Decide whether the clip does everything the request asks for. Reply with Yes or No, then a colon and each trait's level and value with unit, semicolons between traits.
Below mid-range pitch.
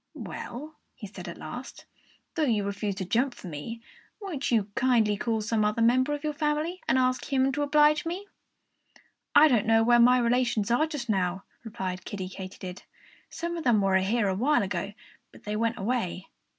No: high, 235 Hz